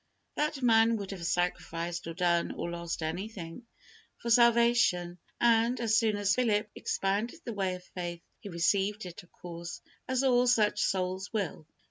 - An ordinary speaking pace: Yes, average, 160 wpm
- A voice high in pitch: Yes, high, 200 Hz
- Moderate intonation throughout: Yes, average, 4.7 semitones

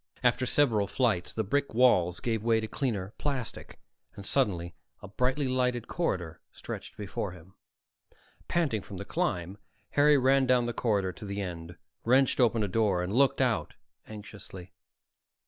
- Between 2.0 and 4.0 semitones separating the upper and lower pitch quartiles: No, average, 5.1 semitones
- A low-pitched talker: Yes, low, 110 Hz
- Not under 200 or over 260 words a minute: No, average, 155 wpm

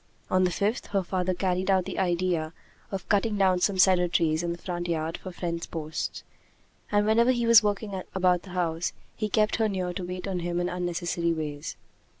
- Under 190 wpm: No, average, 200 wpm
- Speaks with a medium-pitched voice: Yes, medium, 180 Hz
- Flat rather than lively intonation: Yes, narrow, 2.3 semitones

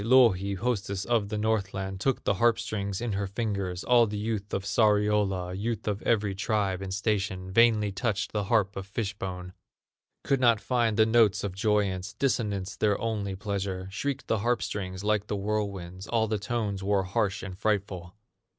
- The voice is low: Yes, low, 100 Hz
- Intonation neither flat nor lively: No, narrow, 2.3 semitones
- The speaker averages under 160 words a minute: No, average, 180 wpm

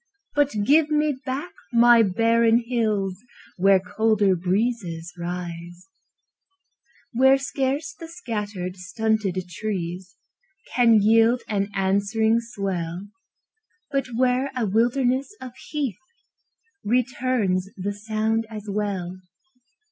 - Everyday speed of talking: No, slow, 100 wpm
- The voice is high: Yes, high, 220 Hz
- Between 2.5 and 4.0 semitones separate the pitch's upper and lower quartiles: No, average, 4.6 semitones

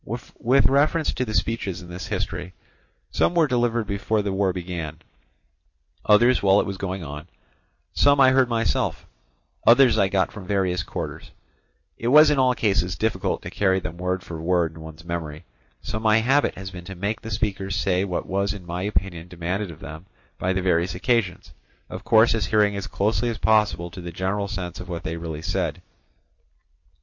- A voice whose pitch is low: Yes, very low, 95 Hz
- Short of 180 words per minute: No, average, 185 wpm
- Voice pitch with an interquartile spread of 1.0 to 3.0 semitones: No, average, 3.9 semitones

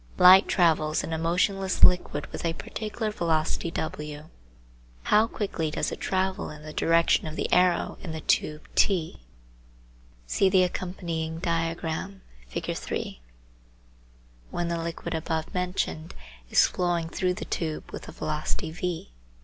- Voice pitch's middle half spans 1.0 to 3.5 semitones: Yes, narrow, 2.4 semitones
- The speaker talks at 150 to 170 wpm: No, average, 140 wpm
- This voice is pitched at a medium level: Yes, medium, 170 Hz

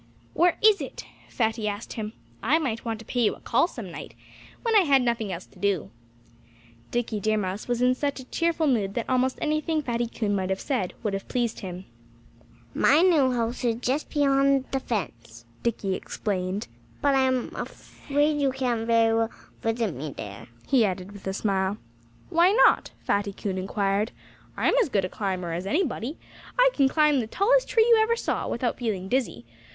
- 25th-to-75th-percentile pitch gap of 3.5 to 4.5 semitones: No, wide, 5.6 semitones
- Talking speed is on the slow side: No, average, 190 wpm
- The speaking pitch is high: Yes, high, 235 Hz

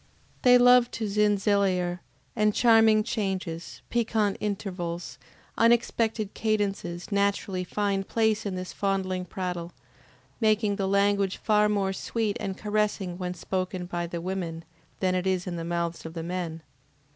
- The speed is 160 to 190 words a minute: No, average, 140 wpm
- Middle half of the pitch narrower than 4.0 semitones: Yes, average, 2.8 semitones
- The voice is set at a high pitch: Yes, high, 195 Hz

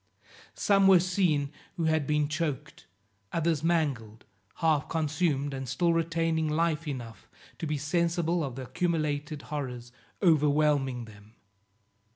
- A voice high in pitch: No, medium, 150 Hz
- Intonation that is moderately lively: Yes, average, 3.1 semitones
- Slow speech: Yes, slow, 125 wpm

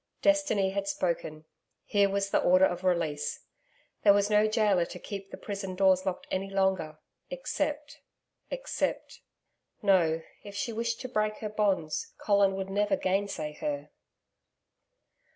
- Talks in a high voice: Yes, high, 195 Hz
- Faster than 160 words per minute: No, average, 140 wpm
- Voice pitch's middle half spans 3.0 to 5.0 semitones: No, narrow, 2.5 semitones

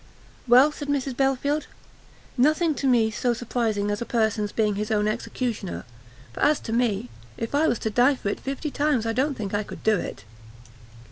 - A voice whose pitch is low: No, high, 240 Hz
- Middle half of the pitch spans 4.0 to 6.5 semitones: Yes, average, 4.4 semitones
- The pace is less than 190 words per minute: No, average, 195 wpm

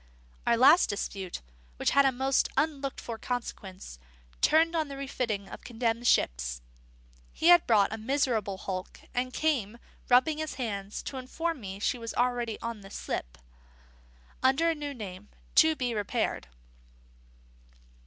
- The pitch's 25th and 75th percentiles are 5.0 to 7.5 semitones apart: Yes, average, 5.3 semitones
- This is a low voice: No, high, 245 Hz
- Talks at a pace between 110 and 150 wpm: Yes, average, 145 wpm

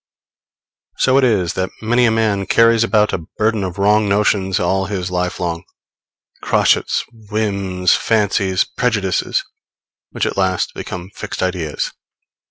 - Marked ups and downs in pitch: No, average, 2.9 semitones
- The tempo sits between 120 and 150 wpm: Yes, slow, 135 wpm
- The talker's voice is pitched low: Yes, low, 100 Hz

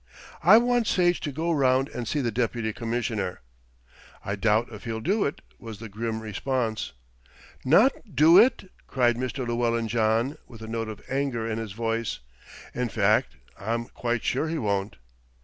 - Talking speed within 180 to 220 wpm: No, average, 165 wpm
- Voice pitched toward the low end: Yes, low, 115 Hz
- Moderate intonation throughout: Yes, average, 3.8 semitones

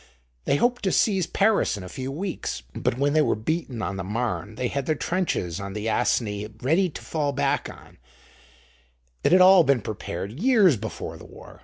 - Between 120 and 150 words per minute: No, average, 195 wpm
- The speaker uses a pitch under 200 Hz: Yes, medium, 140 Hz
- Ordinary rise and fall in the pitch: No, wide, 8.3 semitones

